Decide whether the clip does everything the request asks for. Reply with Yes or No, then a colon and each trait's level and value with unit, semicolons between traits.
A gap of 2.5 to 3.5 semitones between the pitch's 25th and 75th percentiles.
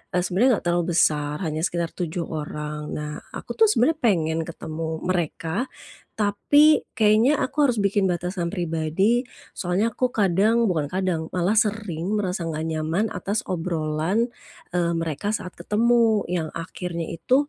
No: average, 4.9 semitones